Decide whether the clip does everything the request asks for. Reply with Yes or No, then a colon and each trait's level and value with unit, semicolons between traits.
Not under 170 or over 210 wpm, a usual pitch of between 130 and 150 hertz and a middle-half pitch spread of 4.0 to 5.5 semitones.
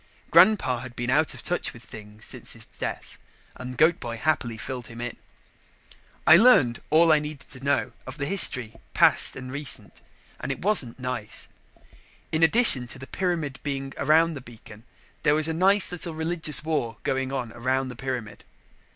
Yes: average, 175 wpm; low, 135 Hz; average, 4.6 semitones